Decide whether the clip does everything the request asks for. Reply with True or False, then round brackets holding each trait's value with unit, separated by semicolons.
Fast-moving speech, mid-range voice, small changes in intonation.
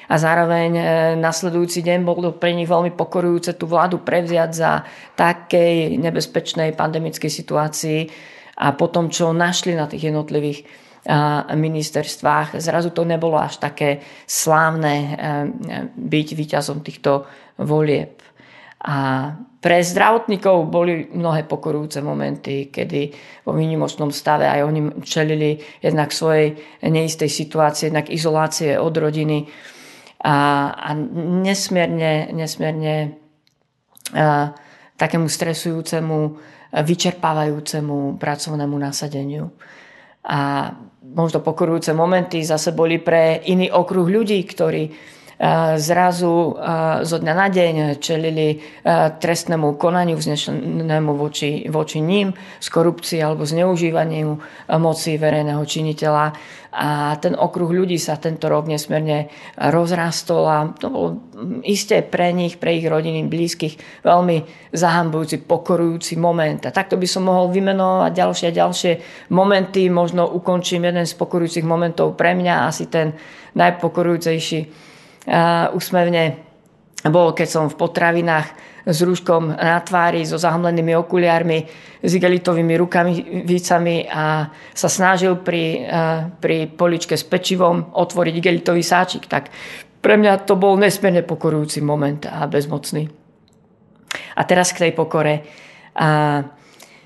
False (115 wpm; 160 Hz; 2.2 semitones)